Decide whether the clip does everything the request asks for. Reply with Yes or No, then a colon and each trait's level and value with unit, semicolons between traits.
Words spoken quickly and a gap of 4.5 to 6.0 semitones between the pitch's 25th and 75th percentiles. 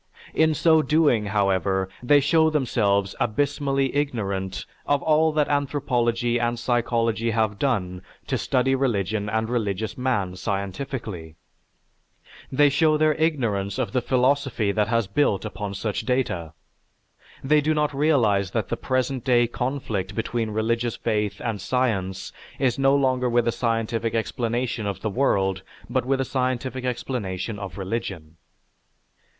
No: average, 140 wpm; average, 4.8 semitones